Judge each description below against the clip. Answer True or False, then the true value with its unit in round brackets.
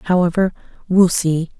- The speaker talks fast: False (115 wpm)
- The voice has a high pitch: False (175 Hz)